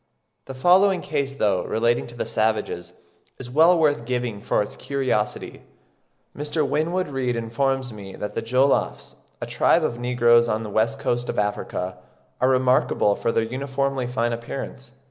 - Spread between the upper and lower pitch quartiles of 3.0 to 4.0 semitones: Yes, average, 3.3 semitones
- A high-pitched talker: No, low, 125 Hz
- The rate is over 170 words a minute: No, average, 155 wpm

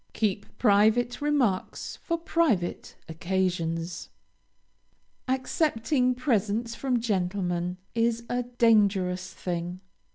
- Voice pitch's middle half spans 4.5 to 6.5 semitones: Yes, average, 5.2 semitones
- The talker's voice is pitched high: Yes, high, 215 Hz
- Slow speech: Yes, slow, 85 wpm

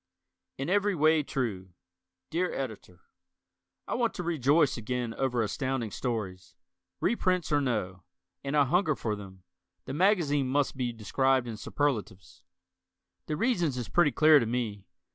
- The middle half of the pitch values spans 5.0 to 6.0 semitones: Yes, wide, 5.6 semitones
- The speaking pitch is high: No, low, 135 Hz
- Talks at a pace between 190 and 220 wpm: No, average, 145 wpm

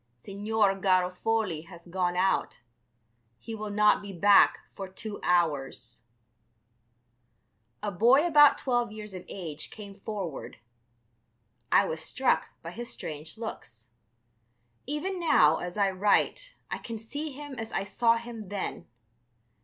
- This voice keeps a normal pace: No, slow, 130 wpm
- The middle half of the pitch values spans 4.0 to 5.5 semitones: Yes, average, 4.3 semitones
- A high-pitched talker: Yes, high, 205 Hz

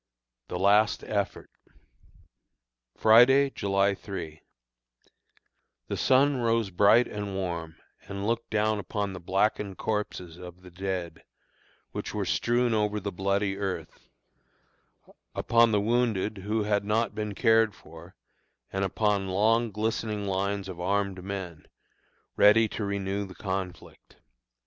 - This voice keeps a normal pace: No, slow, 125 wpm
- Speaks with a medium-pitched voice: No, low, 100 Hz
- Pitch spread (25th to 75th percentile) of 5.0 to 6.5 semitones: No, narrow, 2.4 semitones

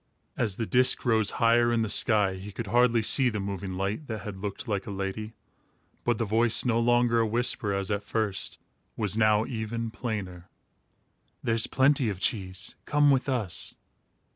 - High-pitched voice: No, low, 110 Hz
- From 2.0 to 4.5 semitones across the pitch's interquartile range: Yes, average, 2.9 semitones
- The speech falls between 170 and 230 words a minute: Yes, average, 175 wpm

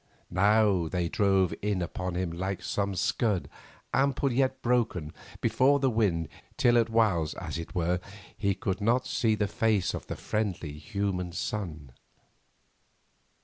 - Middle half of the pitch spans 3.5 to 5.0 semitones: Yes, average, 4.2 semitones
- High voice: No, low, 100 Hz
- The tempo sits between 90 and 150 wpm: Yes, average, 145 wpm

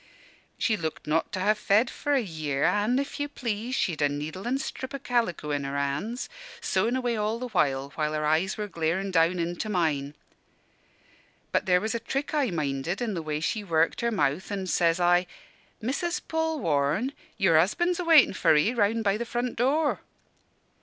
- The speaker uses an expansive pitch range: Yes, wide, 7.2 semitones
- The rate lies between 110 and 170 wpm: No, average, 185 wpm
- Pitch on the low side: No, high, 195 Hz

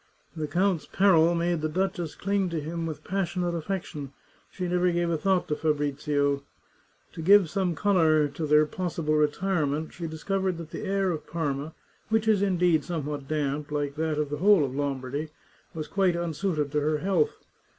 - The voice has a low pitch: No, medium, 160 Hz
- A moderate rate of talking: Yes, average, 175 wpm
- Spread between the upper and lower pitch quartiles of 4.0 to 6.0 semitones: No, average, 3.6 semitones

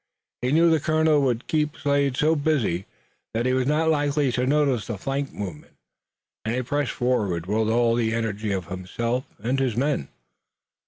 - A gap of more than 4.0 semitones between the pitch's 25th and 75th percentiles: Yes, average, 4.6 semitones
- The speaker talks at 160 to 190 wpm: Yes, average, 175 wpm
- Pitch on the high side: No, low, 125 Hz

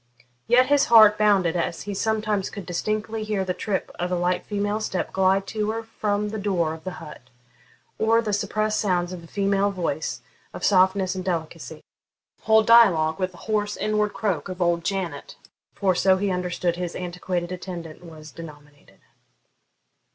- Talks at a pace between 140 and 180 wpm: Yes, average, 170 wpm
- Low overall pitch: No, high, 190 Hz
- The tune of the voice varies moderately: Yes, average, 3.3 semitones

